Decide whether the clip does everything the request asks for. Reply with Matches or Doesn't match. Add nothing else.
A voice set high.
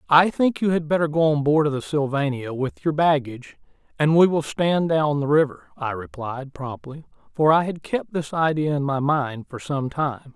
Doesn't match